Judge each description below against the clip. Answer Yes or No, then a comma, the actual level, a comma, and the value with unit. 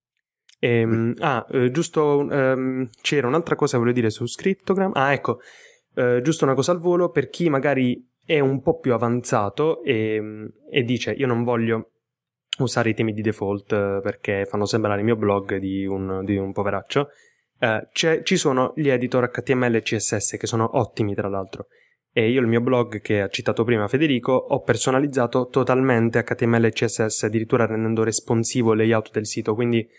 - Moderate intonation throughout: Yes, average, 3.4 semitones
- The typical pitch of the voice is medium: No, low, 120 Hz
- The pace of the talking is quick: Yes, fast, 175 wpm